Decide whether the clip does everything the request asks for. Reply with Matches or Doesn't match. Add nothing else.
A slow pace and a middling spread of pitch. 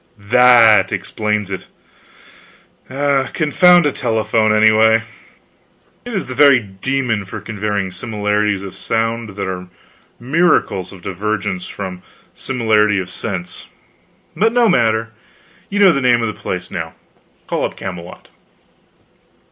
Matches